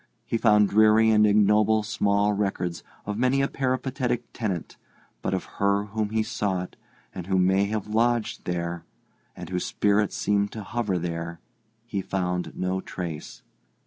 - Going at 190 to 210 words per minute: No, average, 150 wpm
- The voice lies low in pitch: Yes, low, 105 Hz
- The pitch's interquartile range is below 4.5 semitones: Yes, average, 2.8 semitones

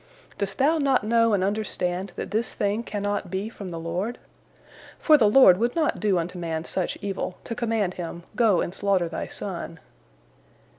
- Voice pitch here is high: Yes, high, 200 Hz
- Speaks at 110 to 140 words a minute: No, average, 180 wpm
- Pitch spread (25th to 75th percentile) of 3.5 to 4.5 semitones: Yes, average, 4.1 semitones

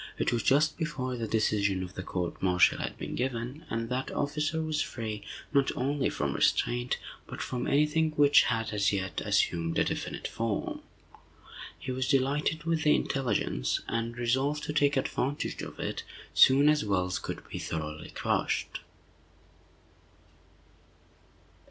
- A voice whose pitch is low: Yes, low, 125 Hz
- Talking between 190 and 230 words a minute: No, average, 150 wpm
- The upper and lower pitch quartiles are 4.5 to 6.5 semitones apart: Yes, wide, 5.6 semitones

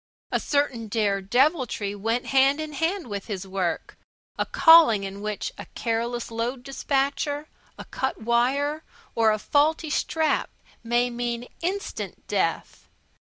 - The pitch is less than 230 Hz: No, high, 245 Hz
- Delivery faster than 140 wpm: No, slow, 135 wpm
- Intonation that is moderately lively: Yes, average, 4.8 semitones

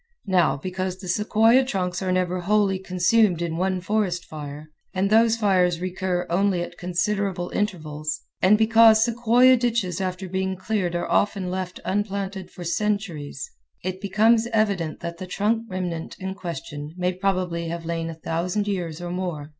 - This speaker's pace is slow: No, average, 155 wpm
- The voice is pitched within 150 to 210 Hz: Yes, medium, 185 Hz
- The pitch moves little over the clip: No, average, 3.0 semitones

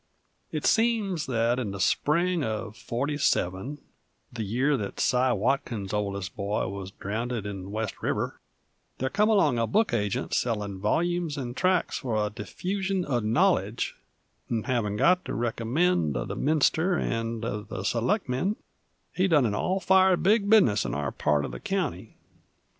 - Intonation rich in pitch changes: Yes, wide, 8.8 semitones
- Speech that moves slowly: No, average, 160 wpm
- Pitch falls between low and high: No, low, 120 Hz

